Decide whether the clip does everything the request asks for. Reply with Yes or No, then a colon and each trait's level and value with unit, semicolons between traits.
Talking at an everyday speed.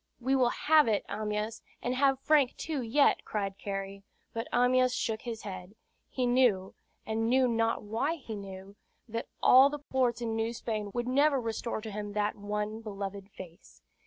Yes: average, 175 wpm